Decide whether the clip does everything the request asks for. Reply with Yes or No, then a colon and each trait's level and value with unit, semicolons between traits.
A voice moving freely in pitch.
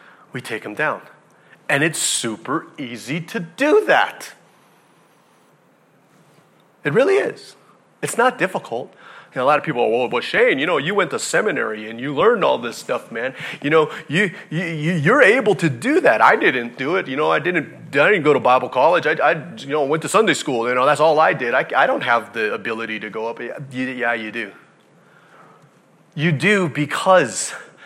Yes: wide, 7.8 semitones